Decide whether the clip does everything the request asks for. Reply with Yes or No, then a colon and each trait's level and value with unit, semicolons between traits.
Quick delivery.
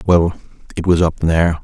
No: average, 185 wpm